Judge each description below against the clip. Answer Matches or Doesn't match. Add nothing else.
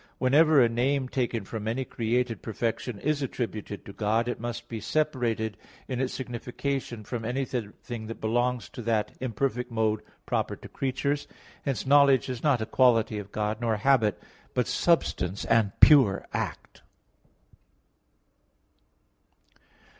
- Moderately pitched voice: Doesn't match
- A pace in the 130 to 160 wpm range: Matches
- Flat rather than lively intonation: Doesn't match